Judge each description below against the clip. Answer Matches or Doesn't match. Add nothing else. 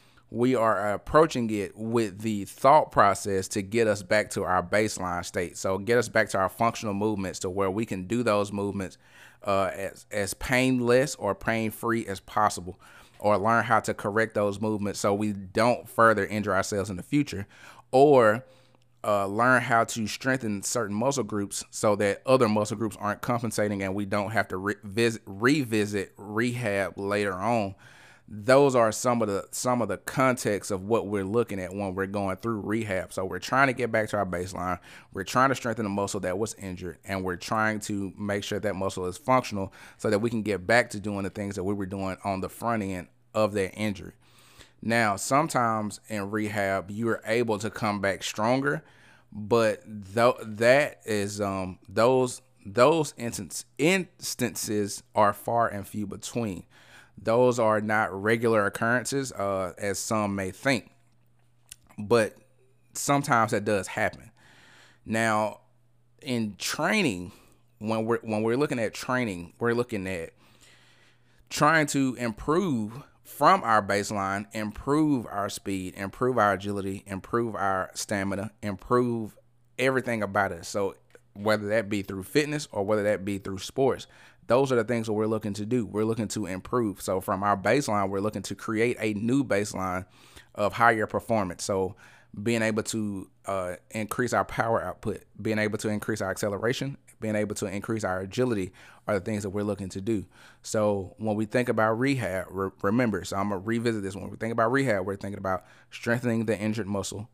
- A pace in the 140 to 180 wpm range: Matches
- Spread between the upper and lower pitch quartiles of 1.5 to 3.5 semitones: Matches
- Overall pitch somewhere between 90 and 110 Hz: Matches